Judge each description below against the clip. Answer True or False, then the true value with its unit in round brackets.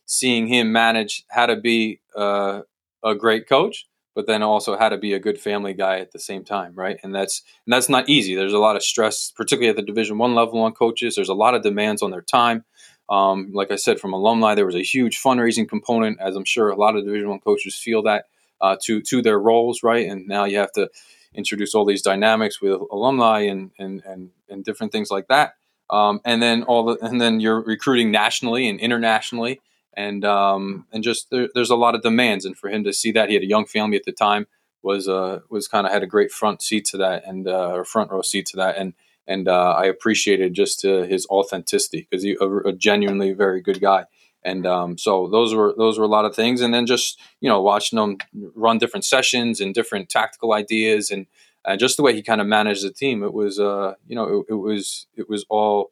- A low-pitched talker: True (105 Hz)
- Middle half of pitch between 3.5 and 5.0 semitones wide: False (2.9 semitones)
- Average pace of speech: False (235 wpm)